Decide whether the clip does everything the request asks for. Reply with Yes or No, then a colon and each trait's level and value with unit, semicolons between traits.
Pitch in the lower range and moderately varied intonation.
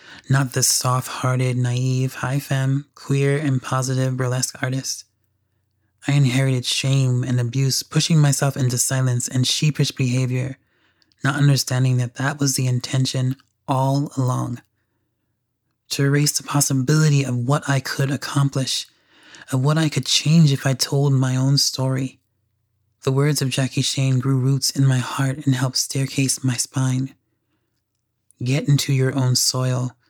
No: low, 130 Hz; narrow, 1.6 semitones